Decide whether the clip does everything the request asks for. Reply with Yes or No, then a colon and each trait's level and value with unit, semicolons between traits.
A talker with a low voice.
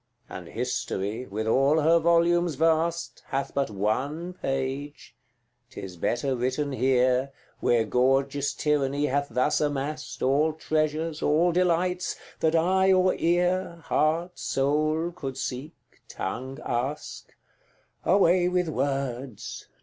No: medium, 145 Hz